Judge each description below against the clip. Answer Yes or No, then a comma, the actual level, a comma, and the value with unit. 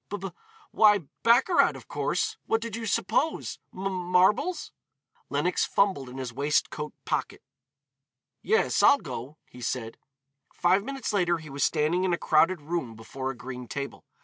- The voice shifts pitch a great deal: Yes, wide, 7.0 semitones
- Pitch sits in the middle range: Yes, medium, 175 Hz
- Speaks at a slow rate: No, average, 155 wpm